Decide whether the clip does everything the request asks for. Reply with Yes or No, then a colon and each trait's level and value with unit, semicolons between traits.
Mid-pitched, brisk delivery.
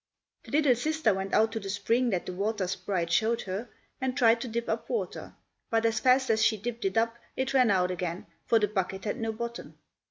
No: high, 225 Hz; fast, 225 wpm